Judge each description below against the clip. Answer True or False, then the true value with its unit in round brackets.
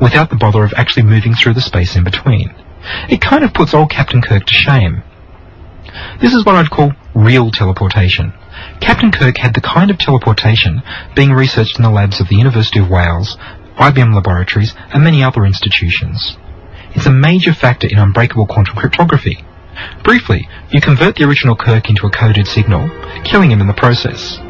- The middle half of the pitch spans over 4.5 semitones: True (5.5 semitones)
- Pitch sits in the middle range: False (110 Hz)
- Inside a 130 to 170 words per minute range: False (180 wpm)